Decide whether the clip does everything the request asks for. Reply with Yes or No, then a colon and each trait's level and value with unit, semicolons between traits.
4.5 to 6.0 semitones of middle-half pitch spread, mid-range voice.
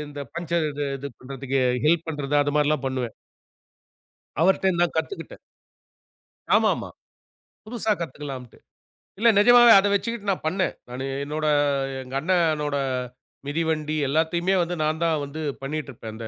No: average, 3.7 semitones; medium, 155 Hz